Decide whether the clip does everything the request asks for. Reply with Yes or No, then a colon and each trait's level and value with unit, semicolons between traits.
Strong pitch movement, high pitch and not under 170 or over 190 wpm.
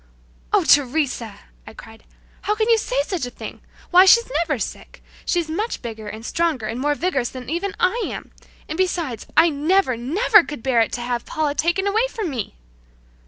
Yes: wide, 6.8 semitones; very high, 300 Hz; average, 185 wpm